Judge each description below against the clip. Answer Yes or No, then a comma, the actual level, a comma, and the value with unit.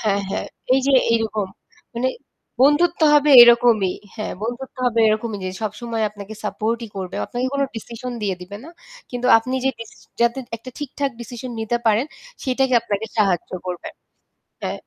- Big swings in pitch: No, average, 3.2 semitones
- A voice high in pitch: Yes, high, 230 Hz